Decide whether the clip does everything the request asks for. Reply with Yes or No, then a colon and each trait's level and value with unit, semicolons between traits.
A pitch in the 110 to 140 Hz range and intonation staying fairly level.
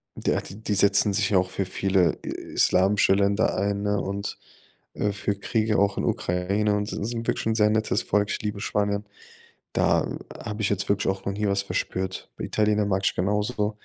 No: low, 100 Hz; narrow, 1.2 semitones